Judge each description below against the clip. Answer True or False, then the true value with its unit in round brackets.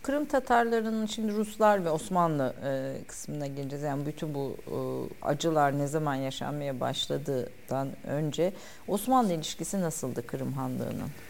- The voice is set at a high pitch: False (150 Hz)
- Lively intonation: True (6.6 semitones)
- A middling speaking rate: True (115 wpm)